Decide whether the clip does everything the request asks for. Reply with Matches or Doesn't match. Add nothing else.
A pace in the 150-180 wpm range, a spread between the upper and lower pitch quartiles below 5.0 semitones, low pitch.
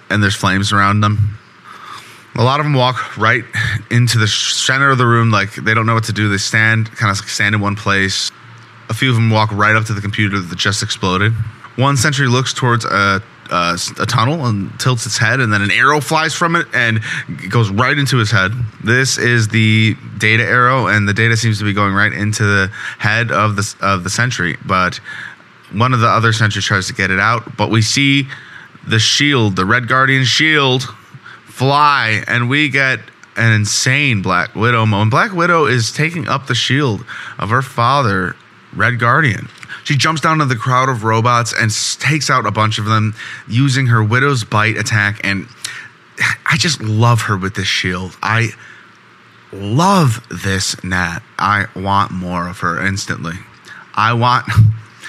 Doesn't match